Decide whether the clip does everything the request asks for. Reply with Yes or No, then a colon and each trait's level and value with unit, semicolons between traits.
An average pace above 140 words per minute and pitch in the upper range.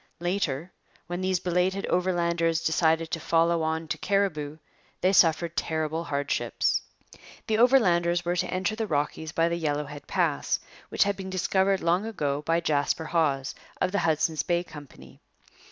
No: average, 155 wpm; medium, 170 Hz